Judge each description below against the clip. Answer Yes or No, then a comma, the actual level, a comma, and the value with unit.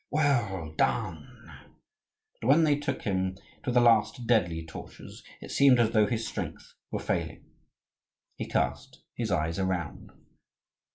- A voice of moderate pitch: No, low, 110 Hz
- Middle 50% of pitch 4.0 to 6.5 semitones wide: Yes, average, 4.8 semitones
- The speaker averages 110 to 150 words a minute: Yes, slow, 135 wpm